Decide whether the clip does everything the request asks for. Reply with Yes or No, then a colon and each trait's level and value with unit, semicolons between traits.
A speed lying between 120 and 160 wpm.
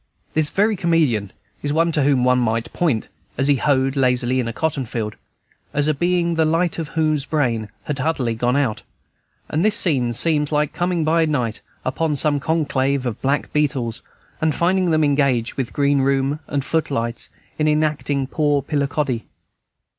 No: average, 175 wpm